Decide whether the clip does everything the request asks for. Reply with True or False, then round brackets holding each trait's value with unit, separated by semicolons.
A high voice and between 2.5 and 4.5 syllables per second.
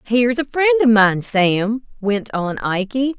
True (230 Hz; 3.9 syllables/s)